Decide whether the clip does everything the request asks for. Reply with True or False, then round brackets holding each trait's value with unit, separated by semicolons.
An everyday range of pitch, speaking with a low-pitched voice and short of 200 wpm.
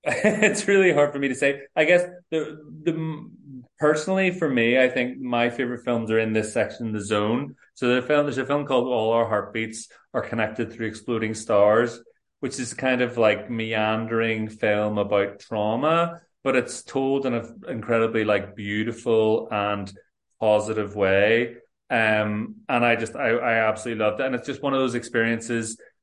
True (3.7 semitones; 115 Hz; 180 wpm)